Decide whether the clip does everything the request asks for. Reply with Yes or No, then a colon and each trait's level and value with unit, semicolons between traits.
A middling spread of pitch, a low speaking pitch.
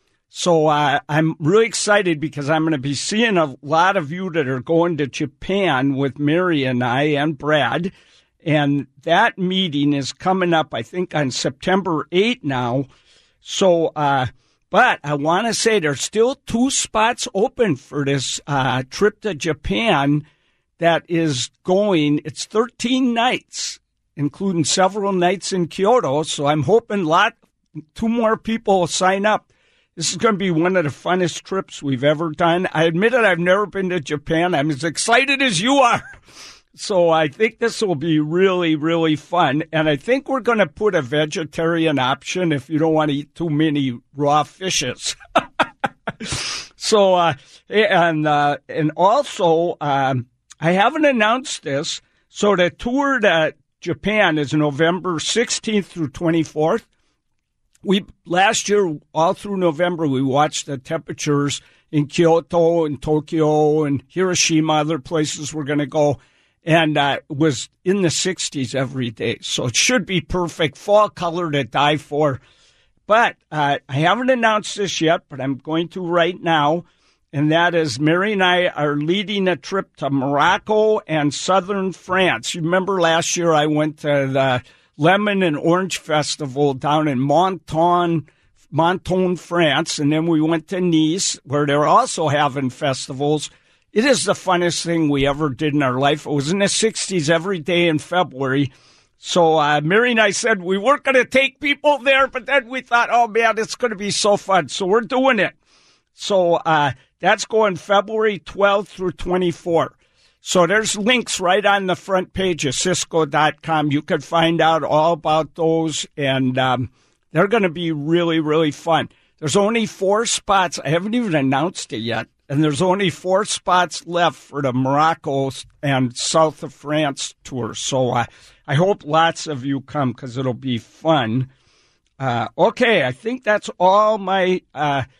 No: average, 4.4 semitones; medium, 165 Hz